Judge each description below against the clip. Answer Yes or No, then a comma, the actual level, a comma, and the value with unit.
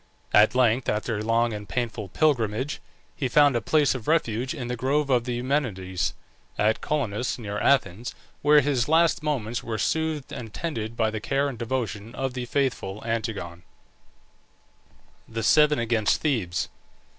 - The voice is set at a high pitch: No, low, 120 Hz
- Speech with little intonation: No, average, 4.3 semitones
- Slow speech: No, average, 155 wpm